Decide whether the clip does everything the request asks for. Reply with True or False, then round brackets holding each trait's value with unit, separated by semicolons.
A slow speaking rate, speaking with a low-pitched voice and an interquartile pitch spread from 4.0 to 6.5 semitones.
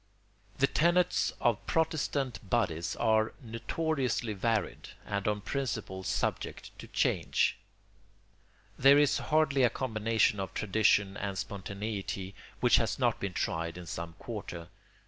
True (125 wpm; 110 Hz; 5.4 semitones)